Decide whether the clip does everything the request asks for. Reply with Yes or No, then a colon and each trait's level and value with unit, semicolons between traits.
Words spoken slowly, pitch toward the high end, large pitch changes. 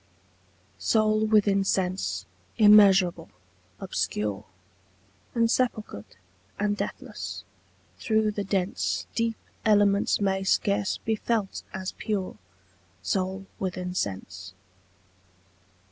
No: slow, 85 wpm; high, 195 Hz; average, 2.8 semitones